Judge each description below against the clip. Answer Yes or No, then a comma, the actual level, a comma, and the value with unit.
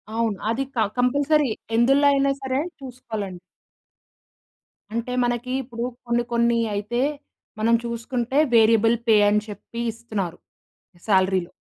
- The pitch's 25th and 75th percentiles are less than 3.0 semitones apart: Yes, narrow, 2.6 semitones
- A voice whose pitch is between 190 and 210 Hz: No, high, 235 Hz